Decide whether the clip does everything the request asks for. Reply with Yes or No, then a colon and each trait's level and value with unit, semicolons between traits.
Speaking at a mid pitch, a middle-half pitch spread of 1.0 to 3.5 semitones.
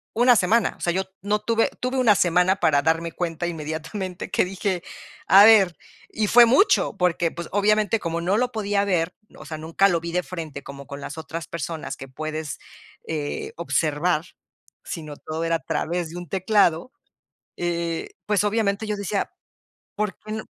No: medium, 175 Hz; average, 4.1 semitones